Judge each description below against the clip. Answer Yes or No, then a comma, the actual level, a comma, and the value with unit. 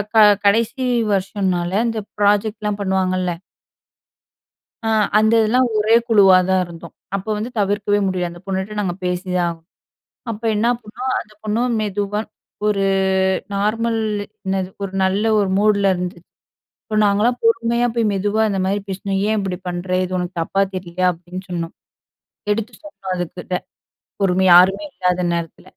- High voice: Yes, high, 195 Hz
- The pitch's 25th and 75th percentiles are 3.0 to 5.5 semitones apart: No, narrow, 2.6 semitones